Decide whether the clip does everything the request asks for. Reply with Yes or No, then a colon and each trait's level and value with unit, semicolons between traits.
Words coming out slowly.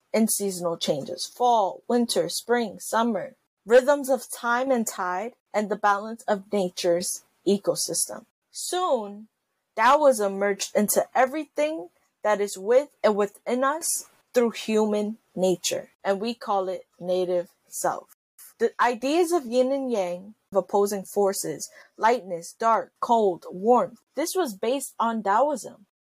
Yes: slow, 130 wpm